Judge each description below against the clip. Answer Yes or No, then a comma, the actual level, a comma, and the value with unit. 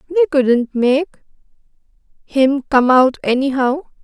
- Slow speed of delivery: Yes, slow, 90 wpm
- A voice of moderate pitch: No, very high, 275 Hz